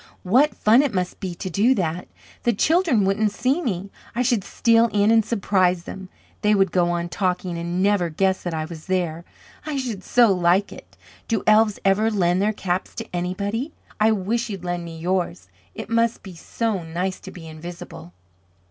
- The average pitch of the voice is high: Yes, high, 195 Hz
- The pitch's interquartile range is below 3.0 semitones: No, average, 4.1 semitones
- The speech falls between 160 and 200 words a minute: Yes, average, 190 wpm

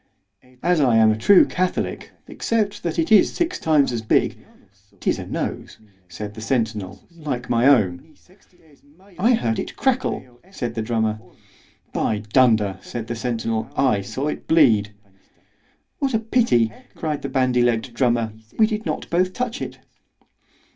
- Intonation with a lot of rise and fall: Yes, wide, 7.8 semitones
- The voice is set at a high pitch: No, low, 125 Hz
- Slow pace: No, average, 145 wpm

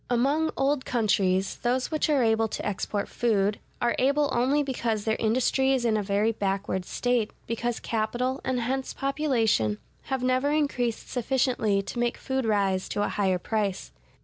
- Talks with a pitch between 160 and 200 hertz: No, high, 240 Hz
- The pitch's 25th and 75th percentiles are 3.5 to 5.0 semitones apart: Yes, average, 4.1 semitones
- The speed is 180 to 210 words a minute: No, average, 165 wpm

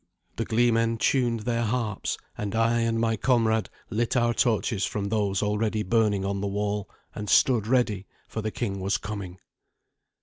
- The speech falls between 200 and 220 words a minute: No, average, 165 wpm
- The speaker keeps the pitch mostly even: Yes, narrow, 2.3 semitones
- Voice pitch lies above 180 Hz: No, low, 110 Hz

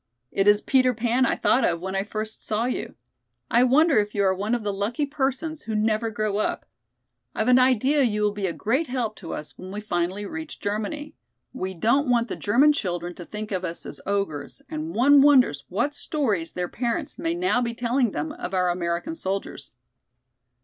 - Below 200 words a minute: No, fast, 205 wpm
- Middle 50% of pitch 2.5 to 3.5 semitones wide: No, average, 5.1 semitones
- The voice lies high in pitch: Yes, high, 220 Hz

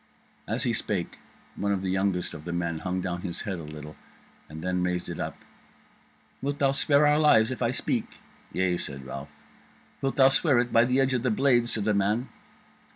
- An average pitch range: No, wide, 6.4 semitones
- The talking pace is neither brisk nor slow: No, fast, 210 wpm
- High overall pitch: No, low, 100 Hz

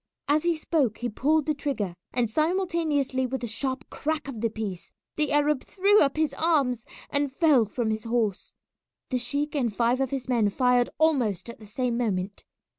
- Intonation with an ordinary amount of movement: Yes, average, 4.4 semitones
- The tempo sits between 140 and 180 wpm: No, average, 190 wpm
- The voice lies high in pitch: Yes, very high, 260 Hz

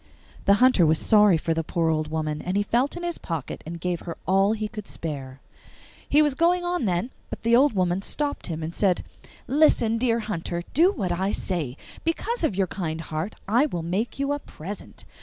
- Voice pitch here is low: No, high, 195 Hz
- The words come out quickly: Yes, fast, 210 wpm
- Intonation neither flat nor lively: No, wide, 7.3 semitones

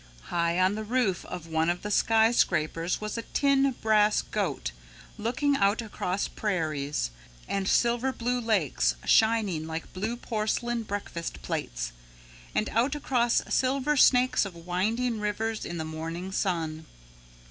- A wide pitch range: Yes, wide, 5.8 semitones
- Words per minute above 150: No, slow, 135 wpm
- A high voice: Yes, high, 210 Hz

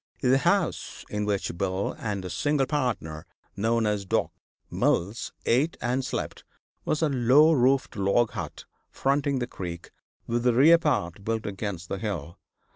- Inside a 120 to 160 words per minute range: Yes, average, 155 wpm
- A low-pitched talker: Yes, low, 115 Hz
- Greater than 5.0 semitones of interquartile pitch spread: Yes, wide, 5.4 semitones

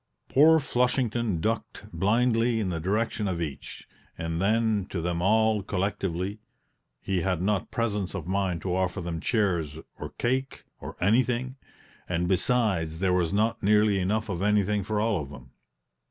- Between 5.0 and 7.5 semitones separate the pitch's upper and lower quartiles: No, average, 3.9 semitones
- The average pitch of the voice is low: Yes, low, 100 Hz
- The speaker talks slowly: No, average, 155 wpm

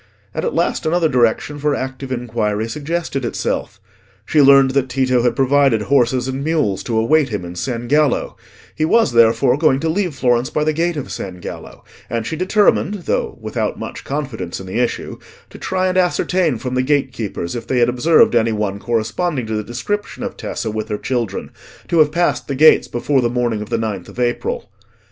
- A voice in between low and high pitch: No, low, 130 Hz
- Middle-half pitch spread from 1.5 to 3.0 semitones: No, average, 4.9 semitones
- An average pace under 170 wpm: No, average, 200 wpm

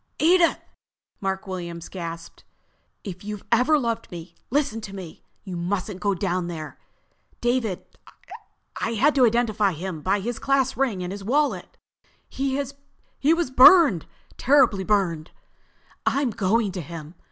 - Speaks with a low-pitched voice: No, high, 205 Hz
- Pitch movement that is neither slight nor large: No, wide, 5.9 semitones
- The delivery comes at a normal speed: No, slow, 130 wpm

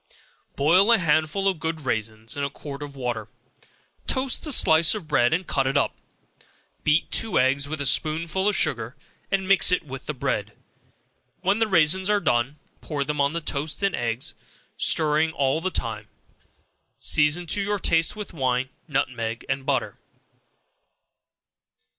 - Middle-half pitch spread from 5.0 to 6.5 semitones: Yes, average, 5.3 semitones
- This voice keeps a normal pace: Yes, average, 160 wpm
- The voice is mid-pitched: Yes, medium, 150 Hz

